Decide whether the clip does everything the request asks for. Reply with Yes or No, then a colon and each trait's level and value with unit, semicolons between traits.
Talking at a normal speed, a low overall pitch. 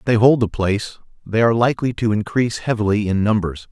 No: fast, 210 wpm; low, 110 Hz